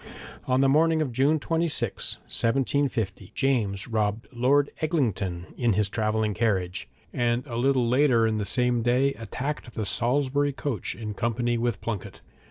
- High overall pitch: No, low, 120 Hz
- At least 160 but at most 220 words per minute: No, average, 150 wpm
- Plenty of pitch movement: No, average, 4.1 semitones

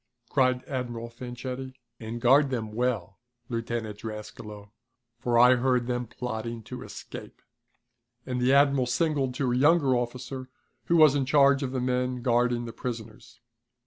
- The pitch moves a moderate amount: No, narrow, 1.9 semitones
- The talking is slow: No, average, 145 wpm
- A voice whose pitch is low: Yes, low, 125 Hz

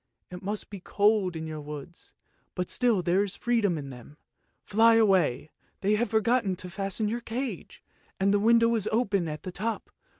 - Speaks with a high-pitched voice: Yes, high, 200 Hz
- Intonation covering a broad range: No, average, 4.0 semitones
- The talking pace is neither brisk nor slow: Yes, average, 185 wpm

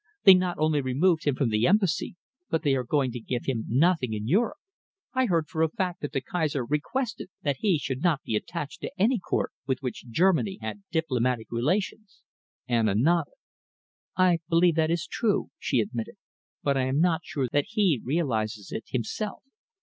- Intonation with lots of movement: Yes, wide, 5.9 semitones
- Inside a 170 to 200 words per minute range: Yes, average, 190 wpm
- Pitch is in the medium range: Yes, medium, 150 Hz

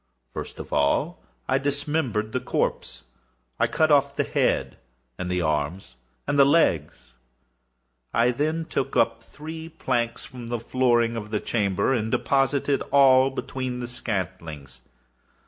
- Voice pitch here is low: Yes, low, 125 Hz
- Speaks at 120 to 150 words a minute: Yes, average, 140 wpm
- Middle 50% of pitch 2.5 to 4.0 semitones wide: No, average, 4.9 semitones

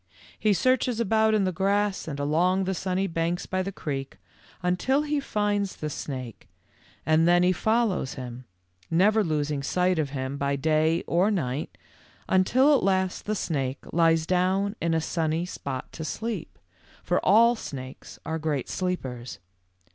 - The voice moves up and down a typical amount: Yes, average, 4.8 semitones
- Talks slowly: No, average, 155 wpm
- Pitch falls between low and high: Yes, medium, 180 Hz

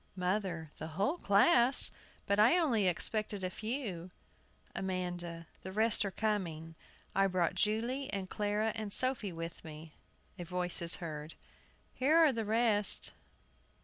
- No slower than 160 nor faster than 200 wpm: No, average, 150 wpm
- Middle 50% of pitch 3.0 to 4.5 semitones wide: Yes, average, 4.1 semitones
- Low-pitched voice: No, high, 200 Hz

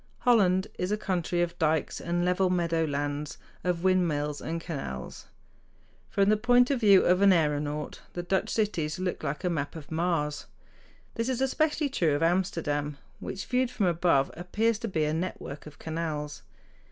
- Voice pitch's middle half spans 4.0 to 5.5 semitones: Yes, average, 4.4 semitones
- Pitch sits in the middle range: Yes, medium, 175 Hz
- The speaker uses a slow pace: No, average, 170 wpm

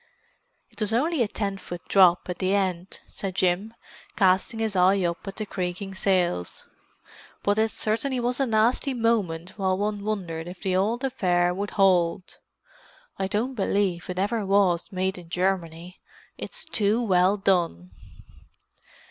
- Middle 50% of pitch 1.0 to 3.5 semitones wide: Yes, average, 3.1 semitones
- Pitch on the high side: Yes, high, 195 Hz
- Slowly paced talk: No, average, 150 wpm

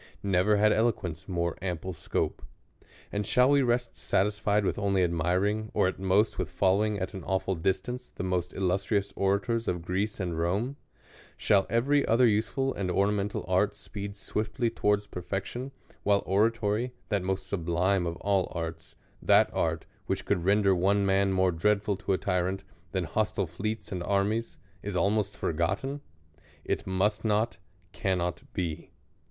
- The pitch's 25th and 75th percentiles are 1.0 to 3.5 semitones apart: Yes, narrow, 2.5 semitones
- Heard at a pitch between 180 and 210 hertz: No, low, 100 Hz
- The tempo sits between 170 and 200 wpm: No, average, 155 wpm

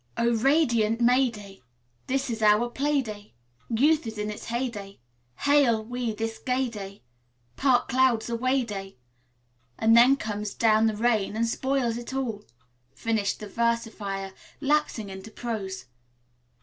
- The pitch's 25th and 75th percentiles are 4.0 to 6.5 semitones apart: No, average, 3.2 semitones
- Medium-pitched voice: No, high, 230 Hz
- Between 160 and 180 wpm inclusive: No, average, 145 wpm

